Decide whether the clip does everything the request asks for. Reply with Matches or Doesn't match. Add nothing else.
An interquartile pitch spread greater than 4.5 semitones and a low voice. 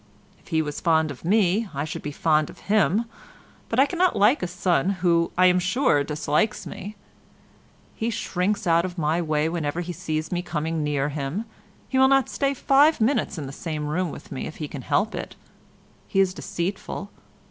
Doesn't match